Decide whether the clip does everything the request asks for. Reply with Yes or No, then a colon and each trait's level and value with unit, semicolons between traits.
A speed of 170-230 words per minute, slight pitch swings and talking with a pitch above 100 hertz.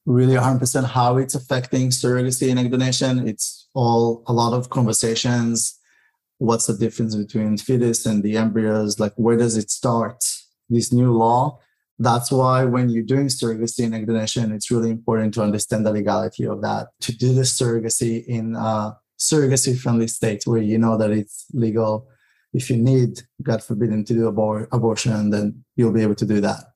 Yes: average, 175 wpm; narrow, 2.1 semitones; low, 115 Hz